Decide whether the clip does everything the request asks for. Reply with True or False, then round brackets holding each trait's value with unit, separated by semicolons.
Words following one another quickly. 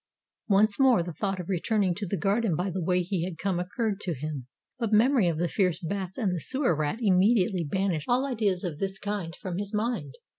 True (220 wpm)